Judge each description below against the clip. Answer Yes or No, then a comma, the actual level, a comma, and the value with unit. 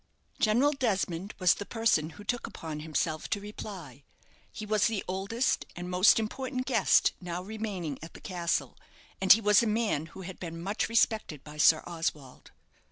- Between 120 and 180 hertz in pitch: No, high, 190 Hz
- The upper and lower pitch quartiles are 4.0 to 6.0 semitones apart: Yes, average, 4.6 semitones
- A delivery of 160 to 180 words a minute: Yes, average, 170 wpm